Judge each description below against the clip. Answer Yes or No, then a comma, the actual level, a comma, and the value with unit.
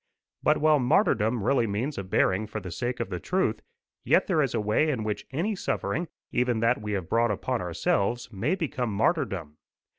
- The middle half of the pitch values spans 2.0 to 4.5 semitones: No, wide, 5.4 semitones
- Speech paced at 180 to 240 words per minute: Yes, average, 190 wpm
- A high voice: No, low, 115 Hz